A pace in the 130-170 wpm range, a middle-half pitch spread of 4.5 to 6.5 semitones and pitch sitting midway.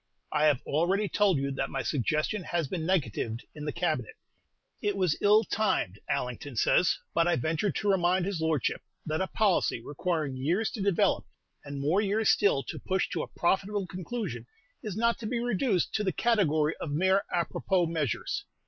No: average, 185 wpm; average, 5.1 semitones; medium, 175 Hz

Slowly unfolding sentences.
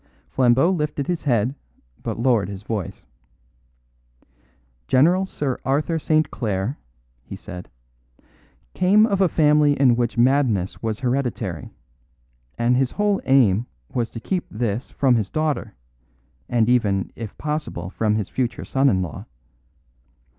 Yes: slow, 130 wpm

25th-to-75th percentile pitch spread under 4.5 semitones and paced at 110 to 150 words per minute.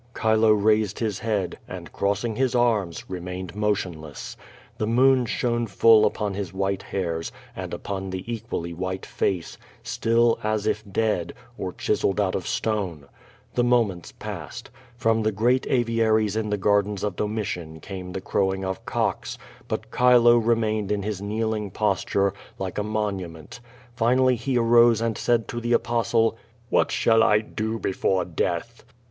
No: average, 3.1 semitones; average, 160 wpm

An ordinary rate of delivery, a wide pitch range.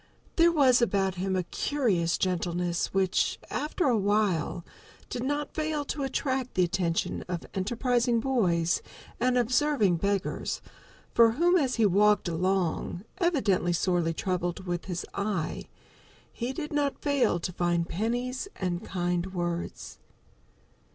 No: slow, 130 wpm; wide, 6.3 semitones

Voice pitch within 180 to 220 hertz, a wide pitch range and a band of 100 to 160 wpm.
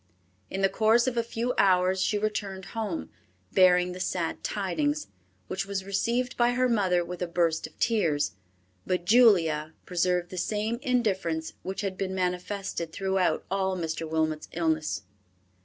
No: high, 190 Hz; average, 3.4 semitones; average, 155 wpm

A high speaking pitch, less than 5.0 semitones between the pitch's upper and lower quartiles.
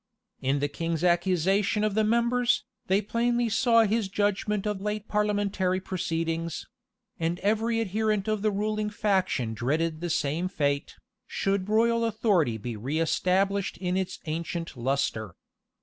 Yes: high, 195 Hz; average, 4.4 semitones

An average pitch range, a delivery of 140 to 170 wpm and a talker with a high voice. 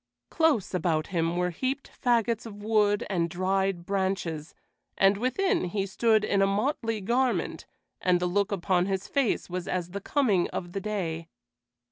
Yes: average, 3.9 semitones; average, 160 wpm; high, 195 Hz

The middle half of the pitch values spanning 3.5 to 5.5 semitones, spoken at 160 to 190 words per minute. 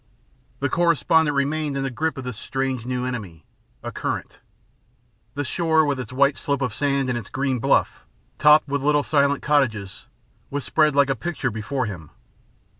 No: narrow, 2.6 semitones; average, 175 wpm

